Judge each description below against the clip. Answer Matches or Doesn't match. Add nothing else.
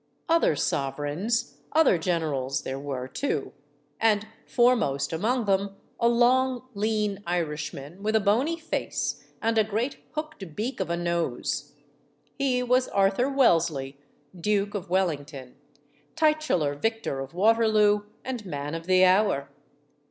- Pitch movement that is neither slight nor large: Doesn't match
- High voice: Matches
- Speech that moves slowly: Matches